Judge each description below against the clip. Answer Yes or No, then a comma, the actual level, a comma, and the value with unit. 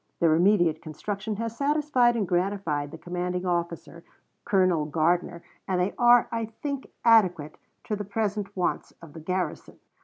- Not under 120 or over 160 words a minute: Yes, average, 150 wpm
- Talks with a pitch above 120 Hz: Yes, medium, 185 Hz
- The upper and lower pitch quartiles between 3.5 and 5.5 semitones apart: Yes, average, 4.4 semitones